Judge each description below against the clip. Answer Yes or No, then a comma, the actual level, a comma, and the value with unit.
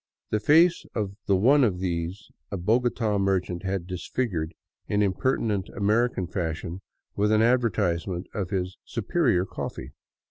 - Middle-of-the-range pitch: No, low, 100 Hz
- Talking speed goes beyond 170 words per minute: No, average, 140 wpm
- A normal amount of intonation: Yes, average, 4.1 semitones